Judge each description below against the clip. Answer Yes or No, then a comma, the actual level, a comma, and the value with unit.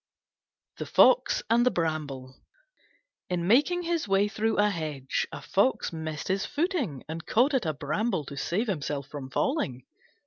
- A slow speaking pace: No, average, 160 wpm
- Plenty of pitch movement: Yes, wide, 8.3 semitones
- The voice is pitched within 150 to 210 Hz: Yes, medium, 185 Hz